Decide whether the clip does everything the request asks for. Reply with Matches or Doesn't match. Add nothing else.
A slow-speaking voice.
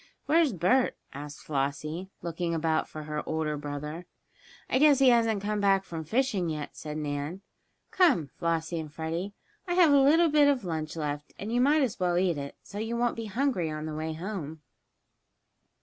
Doesn't match